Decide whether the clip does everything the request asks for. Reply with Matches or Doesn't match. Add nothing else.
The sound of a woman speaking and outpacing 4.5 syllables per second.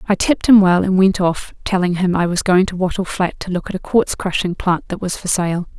Matches